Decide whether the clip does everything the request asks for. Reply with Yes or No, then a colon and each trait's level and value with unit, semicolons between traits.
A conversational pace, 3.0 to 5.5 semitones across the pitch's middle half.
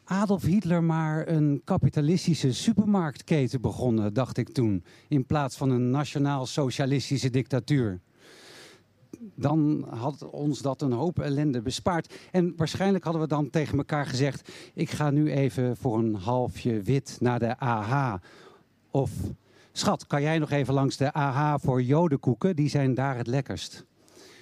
Yes: average, 145 wpm; average, 3.5 semitones